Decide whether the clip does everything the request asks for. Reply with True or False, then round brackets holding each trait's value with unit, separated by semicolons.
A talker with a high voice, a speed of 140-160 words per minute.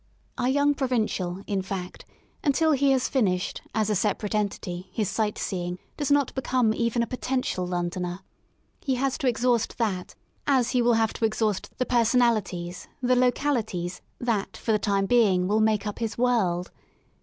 False (220 Hz; 170 wpm)